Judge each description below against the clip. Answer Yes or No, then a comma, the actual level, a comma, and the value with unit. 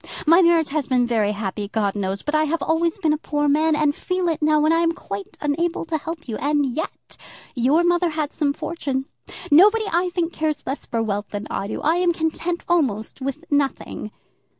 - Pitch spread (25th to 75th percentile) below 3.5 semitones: No, average, 4.4 semitones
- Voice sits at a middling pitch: No, very high, 305 Hz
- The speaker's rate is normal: No, fast, 210 wpm